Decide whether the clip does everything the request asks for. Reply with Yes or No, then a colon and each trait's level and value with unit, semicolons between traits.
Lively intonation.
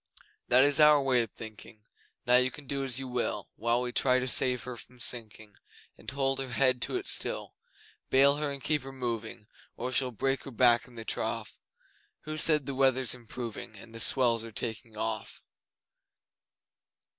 No: narrow, 2.6 semitones